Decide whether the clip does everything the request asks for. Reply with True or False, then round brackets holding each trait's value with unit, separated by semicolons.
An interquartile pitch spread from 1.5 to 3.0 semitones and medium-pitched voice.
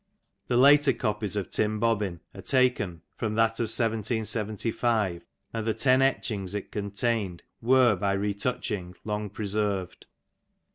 False (2.6 semitones; 110 Hz)